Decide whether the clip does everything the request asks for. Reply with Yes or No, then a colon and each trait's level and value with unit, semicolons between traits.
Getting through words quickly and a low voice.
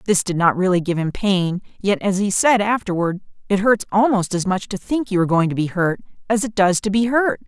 No: fast, 250 wpm; high, 195 Hz